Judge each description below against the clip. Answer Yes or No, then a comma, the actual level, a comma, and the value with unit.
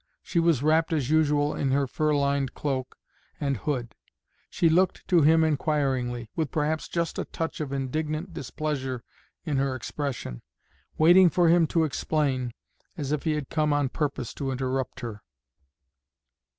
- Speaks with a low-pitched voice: No, medium, 145 Hz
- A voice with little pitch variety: No, average, 3.0 semitones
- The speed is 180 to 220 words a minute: No, average, 155 wpm